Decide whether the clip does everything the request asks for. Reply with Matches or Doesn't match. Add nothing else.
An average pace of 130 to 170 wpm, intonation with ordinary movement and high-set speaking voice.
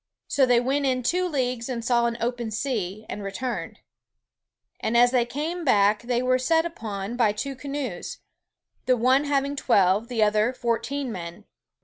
Matches